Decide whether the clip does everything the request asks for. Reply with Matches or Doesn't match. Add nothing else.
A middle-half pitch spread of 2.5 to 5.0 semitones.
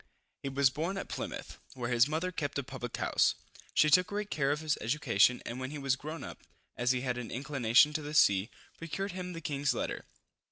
Matches